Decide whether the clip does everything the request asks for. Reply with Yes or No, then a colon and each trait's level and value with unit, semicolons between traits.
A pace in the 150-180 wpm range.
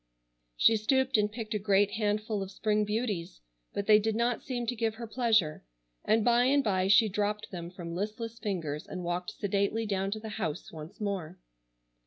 No: average, 190 wpm